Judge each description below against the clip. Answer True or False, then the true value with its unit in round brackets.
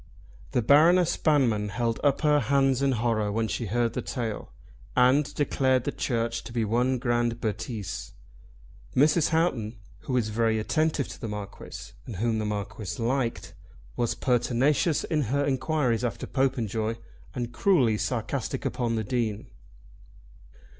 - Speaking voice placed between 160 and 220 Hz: False (120 Hz)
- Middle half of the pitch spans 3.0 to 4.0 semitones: True (3.6 semitones)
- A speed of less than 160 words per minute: True (145 wpm)